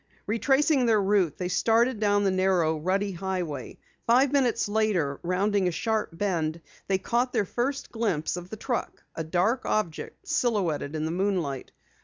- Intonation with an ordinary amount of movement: Yes, average, 4.6 semitones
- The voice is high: Yes, high, 195 Hz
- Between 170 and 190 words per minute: No, average, 160 wpm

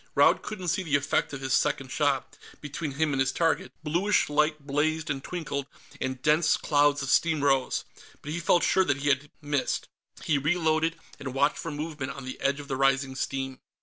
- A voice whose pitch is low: No, medium, 145 Hz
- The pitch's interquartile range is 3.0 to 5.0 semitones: No, narrow, 2.6 semitones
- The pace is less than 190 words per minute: No, average, 200 wpm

